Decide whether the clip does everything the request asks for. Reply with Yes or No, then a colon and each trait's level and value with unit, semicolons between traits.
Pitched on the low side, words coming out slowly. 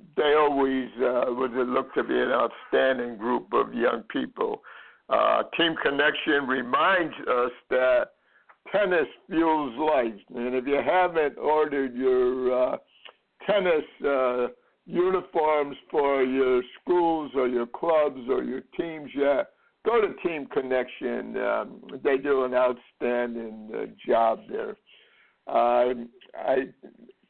Yes: low, 130 Hz; slow, 125 wpm